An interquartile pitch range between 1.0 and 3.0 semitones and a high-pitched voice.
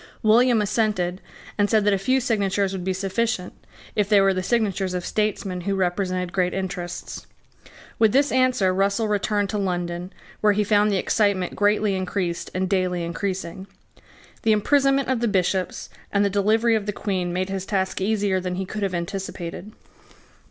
Yes: narrow, 2.5 semitones; high, 195 Hz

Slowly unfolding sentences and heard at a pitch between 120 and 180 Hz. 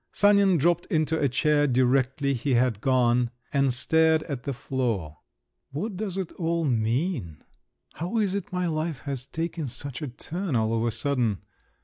No: average, 165 wpm; medium, 140 Hz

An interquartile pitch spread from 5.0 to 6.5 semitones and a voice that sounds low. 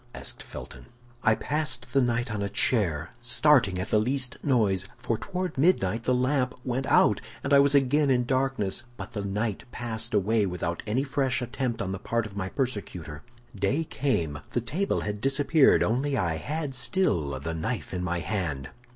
Yes: wide, 5.6 semitones; low, 120 Hz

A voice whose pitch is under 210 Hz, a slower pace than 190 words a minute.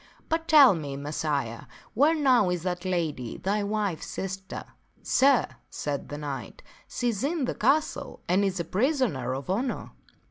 Yes: high, 190 Hz; average, 175 wpm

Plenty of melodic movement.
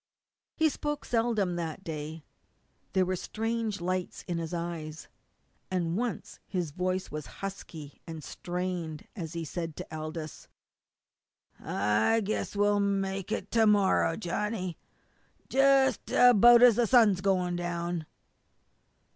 No: average, 4.1 semitones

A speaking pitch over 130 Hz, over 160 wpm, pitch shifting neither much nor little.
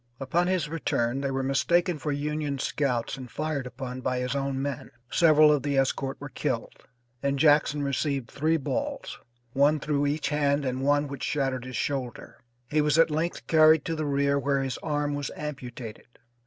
No: medium, 140 Hz; average, 180 wpm; narrow, 2.1 semitones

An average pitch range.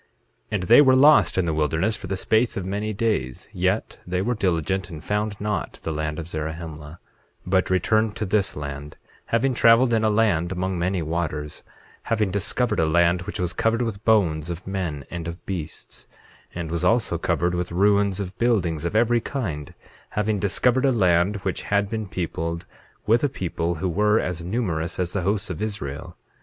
Yes: average, 4.3 semitones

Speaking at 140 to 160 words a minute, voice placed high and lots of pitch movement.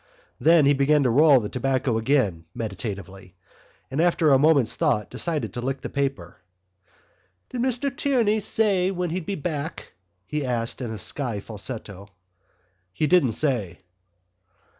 No: average, 145 wpm; low, 135 Hz; wide, 6.6 semitones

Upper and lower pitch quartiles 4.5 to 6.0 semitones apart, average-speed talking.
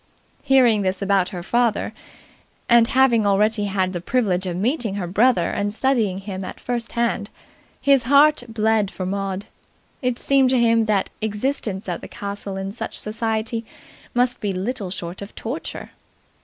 No: average, 3.8 semitones; average, 160 wpm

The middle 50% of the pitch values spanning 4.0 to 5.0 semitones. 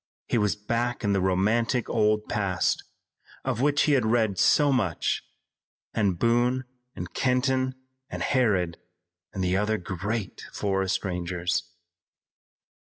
Yes: average, 4.4 semitones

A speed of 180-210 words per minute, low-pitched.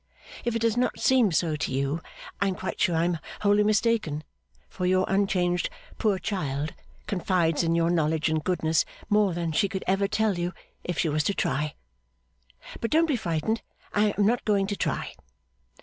No: average, 185 wpm; medium, 185 Hz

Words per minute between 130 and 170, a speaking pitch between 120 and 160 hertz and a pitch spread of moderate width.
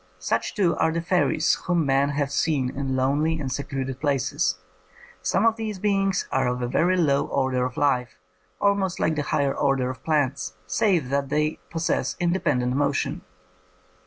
Yes: average, 165 wpm; medium, 140 Hz; average, 4.2 semitones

